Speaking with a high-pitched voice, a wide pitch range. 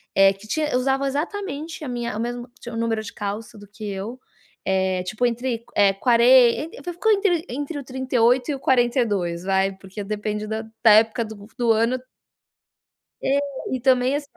No: high, 235 Hz; average, 4.0 semitones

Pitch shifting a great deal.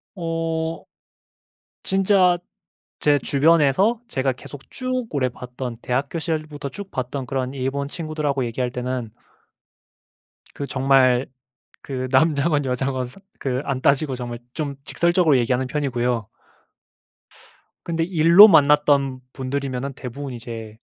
No: average, 3.7 semitones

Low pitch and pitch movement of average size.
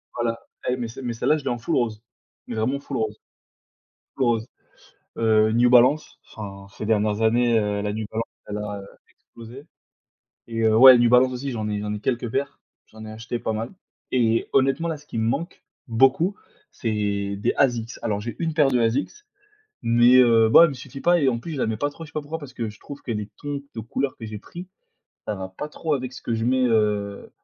Yes: low, 115 Hz; average, 3.4 semitones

